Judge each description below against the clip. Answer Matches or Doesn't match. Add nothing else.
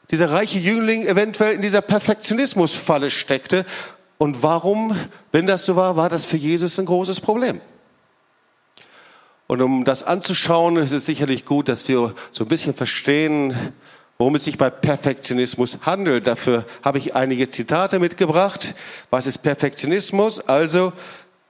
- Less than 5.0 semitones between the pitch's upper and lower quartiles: Doesn't match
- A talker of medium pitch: Matches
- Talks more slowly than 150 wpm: Matches